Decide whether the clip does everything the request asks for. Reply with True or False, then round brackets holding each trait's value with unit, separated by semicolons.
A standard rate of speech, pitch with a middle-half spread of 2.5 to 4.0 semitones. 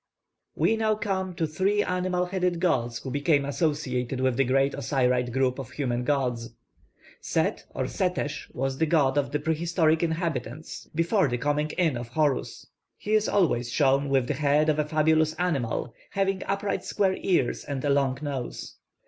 False (170 wpm; 4.8 semitones)